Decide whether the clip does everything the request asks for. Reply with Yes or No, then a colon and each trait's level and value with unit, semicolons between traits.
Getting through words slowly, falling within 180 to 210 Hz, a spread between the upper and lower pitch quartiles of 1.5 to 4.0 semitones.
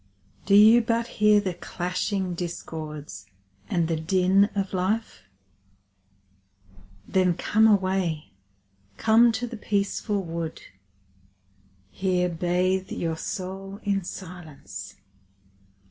Yes: slow, 100 wpm; medium, 185 Hz; average, 3.2 semitones